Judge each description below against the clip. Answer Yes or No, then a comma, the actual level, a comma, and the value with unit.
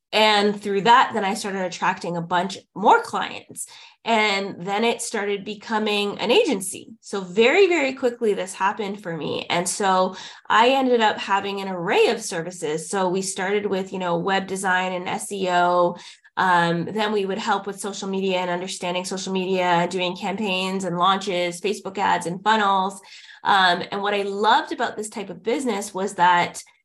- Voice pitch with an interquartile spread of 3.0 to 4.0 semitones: No, narrow, 2.5 semitones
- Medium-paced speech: Yes, average, 175 wpm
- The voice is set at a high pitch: Yes, high, 195 Hz